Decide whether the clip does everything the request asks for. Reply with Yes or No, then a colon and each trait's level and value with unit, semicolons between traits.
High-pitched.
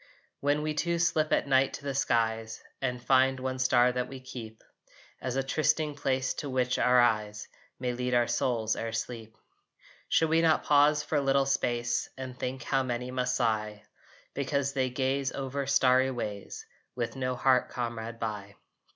No: low, 130 Hz